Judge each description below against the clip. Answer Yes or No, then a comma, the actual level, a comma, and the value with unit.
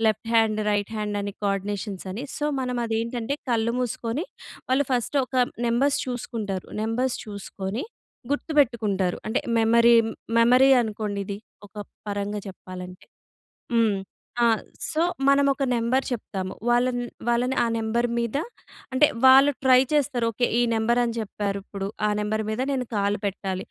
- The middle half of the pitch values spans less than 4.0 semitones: Yes, average, 3.5 semitones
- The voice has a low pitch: No, high, 230 Hz